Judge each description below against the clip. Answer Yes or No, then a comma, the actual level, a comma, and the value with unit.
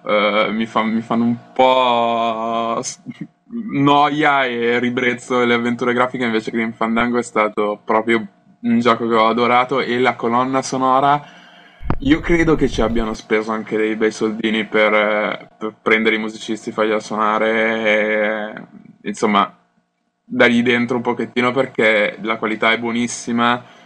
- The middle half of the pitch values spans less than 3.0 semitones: Yes, narrow, 2.4 semitones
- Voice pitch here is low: Yes, low, 115 Hz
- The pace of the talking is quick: No, average, 145 wpm